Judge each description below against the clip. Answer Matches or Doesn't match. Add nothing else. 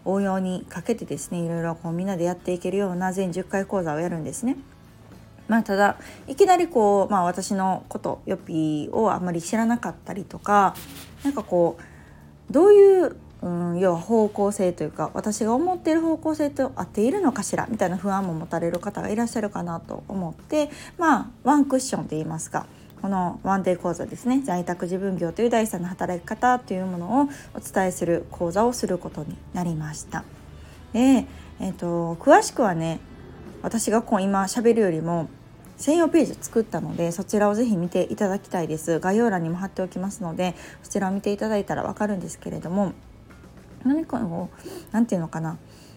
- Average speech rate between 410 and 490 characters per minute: Doesn't match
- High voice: Matches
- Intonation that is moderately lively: Matches